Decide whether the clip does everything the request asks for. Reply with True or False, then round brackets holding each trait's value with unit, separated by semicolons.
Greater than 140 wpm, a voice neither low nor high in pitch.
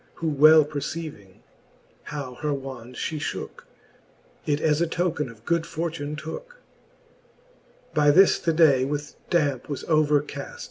False (135 wpm; 150 Hz)